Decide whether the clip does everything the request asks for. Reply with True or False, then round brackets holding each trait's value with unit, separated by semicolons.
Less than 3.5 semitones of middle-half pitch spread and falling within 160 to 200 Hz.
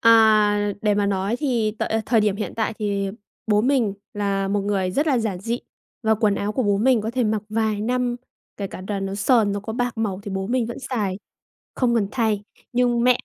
False (2.8 semitones; 215 Hz)